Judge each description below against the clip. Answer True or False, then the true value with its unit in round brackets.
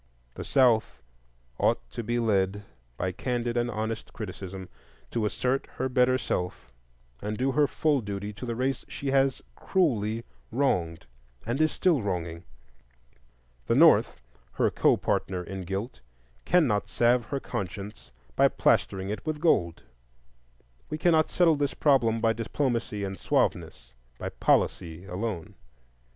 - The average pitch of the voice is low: True (110 Hz)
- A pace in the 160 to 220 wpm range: False (135 wpm)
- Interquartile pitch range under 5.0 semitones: False (5.5 semitones)